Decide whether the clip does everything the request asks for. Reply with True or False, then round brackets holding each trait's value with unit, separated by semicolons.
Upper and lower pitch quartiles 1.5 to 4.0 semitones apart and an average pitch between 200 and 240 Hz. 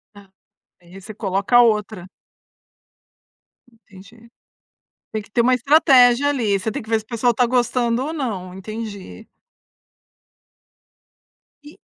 True (3.4 semitones; 225 Hz)